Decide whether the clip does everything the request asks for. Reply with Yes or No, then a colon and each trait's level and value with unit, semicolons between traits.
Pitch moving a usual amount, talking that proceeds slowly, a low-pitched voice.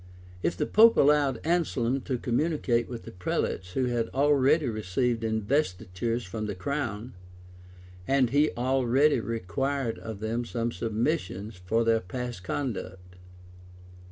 Yes: average, 4.0 semitones; slow, 130 wpm; low, 120 Hz